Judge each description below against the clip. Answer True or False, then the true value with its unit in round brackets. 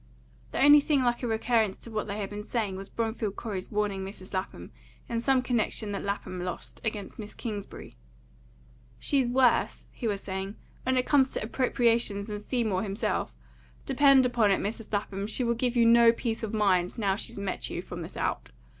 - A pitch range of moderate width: True (3.2 semitones)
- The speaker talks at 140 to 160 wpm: False (195 wpm)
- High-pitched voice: True (220 Hz)